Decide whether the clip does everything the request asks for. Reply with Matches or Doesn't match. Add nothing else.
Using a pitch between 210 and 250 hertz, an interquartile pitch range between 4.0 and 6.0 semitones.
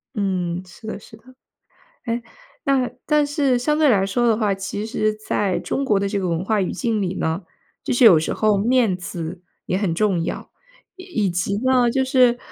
Matches